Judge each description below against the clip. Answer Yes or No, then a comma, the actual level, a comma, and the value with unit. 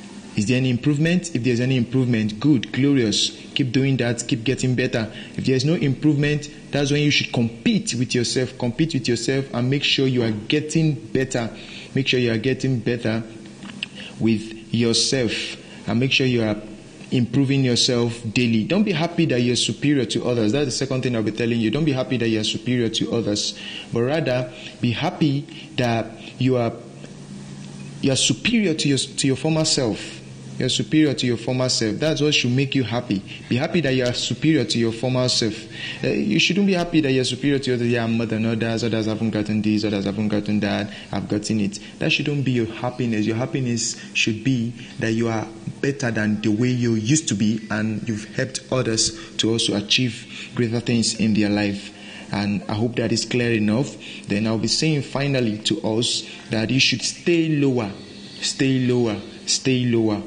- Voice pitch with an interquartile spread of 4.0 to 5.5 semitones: No, average, 3.4 semitones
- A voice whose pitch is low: Yes, low, 120 Hz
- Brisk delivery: No, average, 195 wpm